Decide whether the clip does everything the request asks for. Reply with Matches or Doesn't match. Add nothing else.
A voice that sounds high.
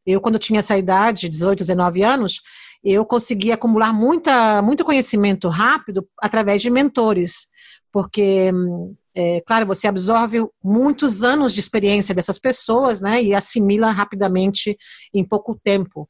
Matches